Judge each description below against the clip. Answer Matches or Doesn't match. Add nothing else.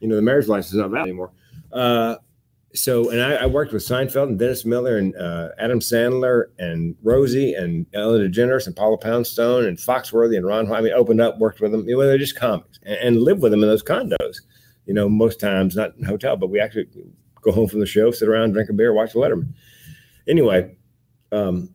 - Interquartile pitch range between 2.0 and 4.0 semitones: Matches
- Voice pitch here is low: Matches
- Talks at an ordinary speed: Doesn't match